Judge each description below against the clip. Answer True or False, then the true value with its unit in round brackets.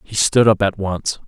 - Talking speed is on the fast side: True (235 wpm)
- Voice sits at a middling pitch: False (100 Hz)